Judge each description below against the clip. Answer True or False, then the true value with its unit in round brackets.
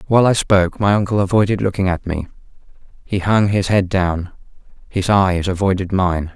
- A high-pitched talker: False (95 Hz)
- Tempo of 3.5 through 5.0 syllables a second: False (5.4 syllables/s)